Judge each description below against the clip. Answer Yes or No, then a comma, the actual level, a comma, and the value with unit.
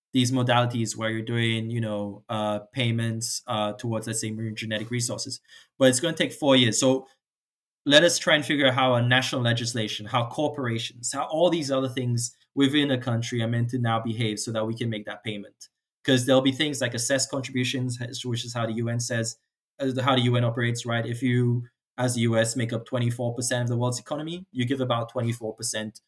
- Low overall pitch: Yes, low, 120 Hz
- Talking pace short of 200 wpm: No, fast, 205 wpm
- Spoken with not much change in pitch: Yes, narrow, 2.3 semitones